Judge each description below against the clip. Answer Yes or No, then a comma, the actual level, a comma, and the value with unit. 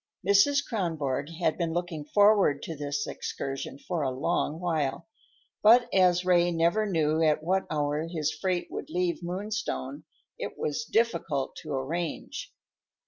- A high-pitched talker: No, medium, 165 Hz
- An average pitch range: Yes, average, 3.7 semitones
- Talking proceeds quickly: No, average, 140 wpm